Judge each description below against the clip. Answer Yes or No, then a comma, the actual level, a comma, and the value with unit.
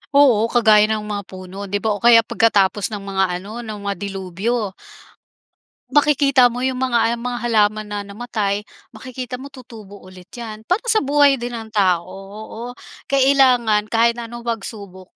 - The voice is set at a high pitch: Yes, high, 225 Hz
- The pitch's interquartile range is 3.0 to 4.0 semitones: Yes, average, 3.3 semitones